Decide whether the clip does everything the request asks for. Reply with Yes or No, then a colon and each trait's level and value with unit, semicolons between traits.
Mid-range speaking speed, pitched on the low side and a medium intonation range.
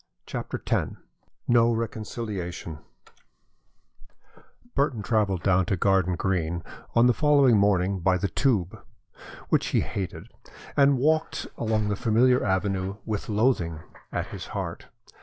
No: slow, 120 wpm; low, 105 Hz; average, 4.1 semitones